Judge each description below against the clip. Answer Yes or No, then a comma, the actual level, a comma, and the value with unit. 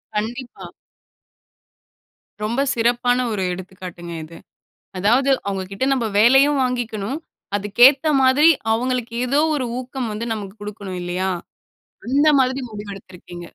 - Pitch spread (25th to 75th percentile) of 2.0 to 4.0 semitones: No, average, 4.8 semitones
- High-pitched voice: Yes, high, 230 Hz